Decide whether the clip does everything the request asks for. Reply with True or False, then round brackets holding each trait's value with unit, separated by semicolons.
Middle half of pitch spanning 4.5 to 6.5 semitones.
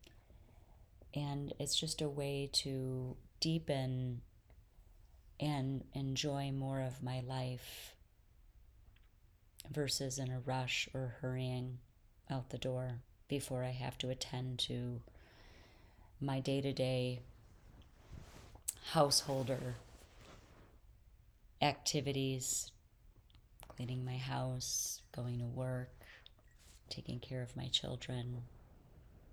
False (3.3 semitones)